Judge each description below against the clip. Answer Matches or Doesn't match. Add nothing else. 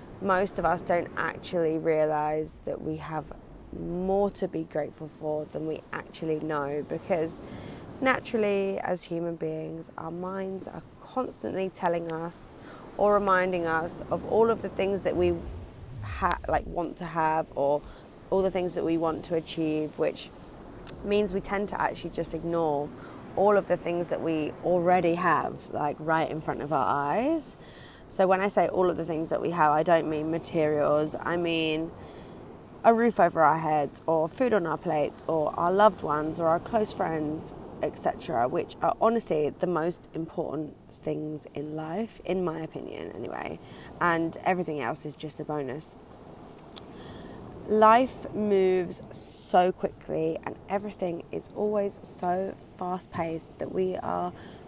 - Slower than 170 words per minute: Matches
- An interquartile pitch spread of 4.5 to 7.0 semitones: Doesn't match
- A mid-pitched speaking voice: Matches